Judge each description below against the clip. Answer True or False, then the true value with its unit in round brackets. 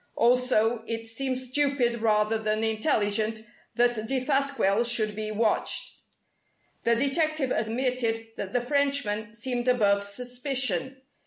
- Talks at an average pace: False (110 wpm)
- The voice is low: False (235 Hz)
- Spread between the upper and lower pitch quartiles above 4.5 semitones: False (3.1 semitones)